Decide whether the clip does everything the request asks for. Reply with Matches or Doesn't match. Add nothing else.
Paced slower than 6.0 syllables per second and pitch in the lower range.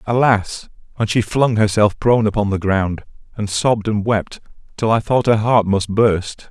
Matches